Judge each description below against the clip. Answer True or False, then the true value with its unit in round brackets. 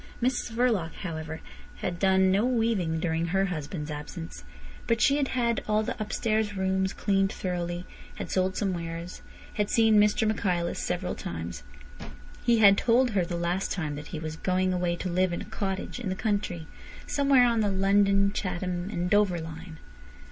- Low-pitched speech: False (190 Hz)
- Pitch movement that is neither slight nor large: True (3.5 semitones)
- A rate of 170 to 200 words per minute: True (175 wpm)